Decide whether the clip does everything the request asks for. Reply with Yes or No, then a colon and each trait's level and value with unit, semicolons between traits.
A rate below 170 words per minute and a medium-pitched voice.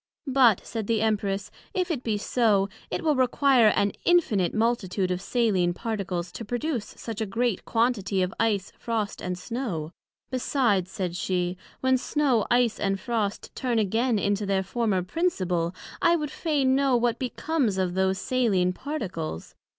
No: average, 160 wpm; high, 220 Hz